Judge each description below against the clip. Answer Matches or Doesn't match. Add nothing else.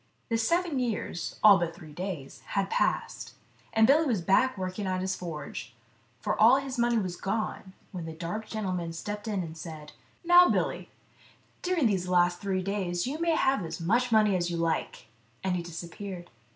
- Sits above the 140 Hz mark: Matches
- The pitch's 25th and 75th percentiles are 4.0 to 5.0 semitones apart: Matches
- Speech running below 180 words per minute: Doesn't match